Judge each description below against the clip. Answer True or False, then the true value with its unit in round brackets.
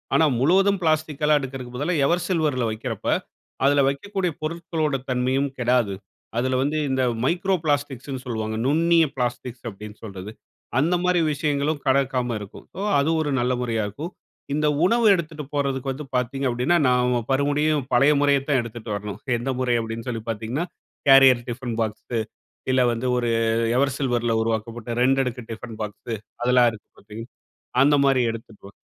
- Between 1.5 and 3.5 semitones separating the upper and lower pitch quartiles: False (3.9 semitones)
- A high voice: False (130 Hz)